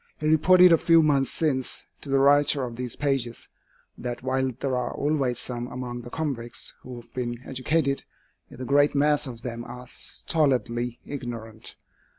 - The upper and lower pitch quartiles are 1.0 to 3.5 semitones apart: Yes, average, 3.0 semitones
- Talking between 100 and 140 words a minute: No, average, 165 wpm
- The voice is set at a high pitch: No, low, 130 Hz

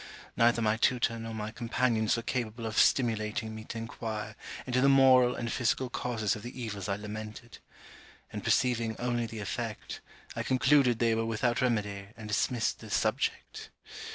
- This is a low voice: Yes, low, 115 Hz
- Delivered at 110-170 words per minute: Yes, average, 165 wpm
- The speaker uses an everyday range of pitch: No, narrow, 2.0 semitones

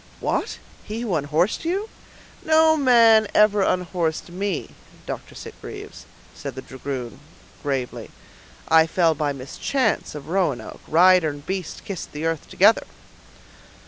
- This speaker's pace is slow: Yes, slow, 125 wpm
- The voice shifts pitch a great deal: Yes, wide, 6.1 semitones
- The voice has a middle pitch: Yes, medium, 175 Hz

